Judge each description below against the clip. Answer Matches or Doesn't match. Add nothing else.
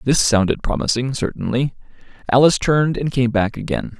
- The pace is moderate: Matches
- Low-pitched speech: Matches